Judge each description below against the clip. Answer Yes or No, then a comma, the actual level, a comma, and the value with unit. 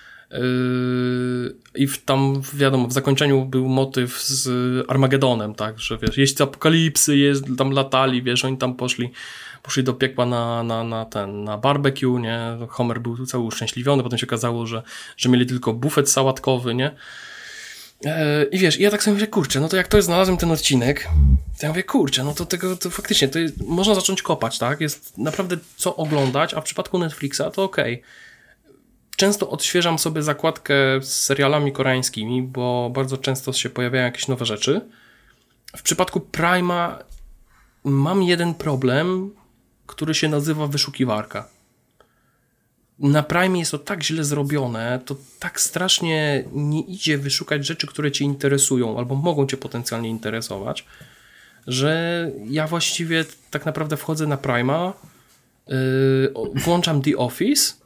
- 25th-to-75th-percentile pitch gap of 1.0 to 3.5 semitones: No, average, 4.4 semitones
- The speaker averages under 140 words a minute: No, average, 155 wpm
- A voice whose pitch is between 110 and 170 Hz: Yes, medium, 140 Hz